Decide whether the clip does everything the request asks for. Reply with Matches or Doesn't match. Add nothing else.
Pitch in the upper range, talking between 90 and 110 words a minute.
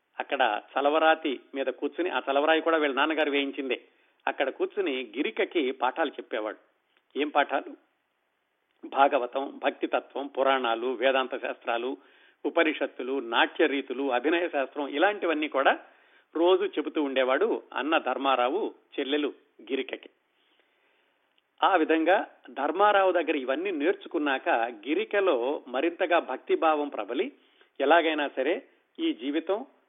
Doesn't match